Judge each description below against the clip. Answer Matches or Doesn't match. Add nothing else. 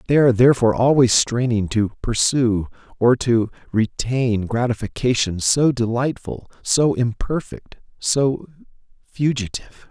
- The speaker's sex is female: Doesn't match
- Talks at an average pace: Doesn't match